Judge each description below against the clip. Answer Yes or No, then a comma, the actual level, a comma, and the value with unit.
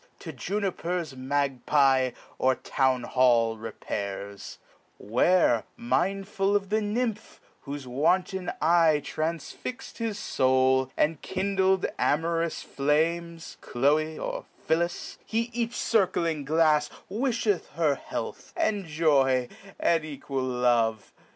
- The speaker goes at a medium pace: No, slow, 105 wpm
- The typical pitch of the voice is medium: Yes, medium, 155 Hz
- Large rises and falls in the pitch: Yes, wide, 6.3 semitones